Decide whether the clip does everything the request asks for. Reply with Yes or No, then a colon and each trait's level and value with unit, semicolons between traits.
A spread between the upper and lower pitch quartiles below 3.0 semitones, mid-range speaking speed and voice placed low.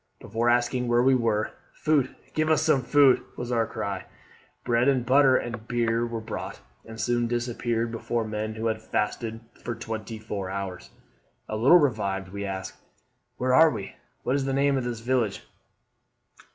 Yes: narrow, 2.6 semitones; average, 170 wpm; low, 120 Hz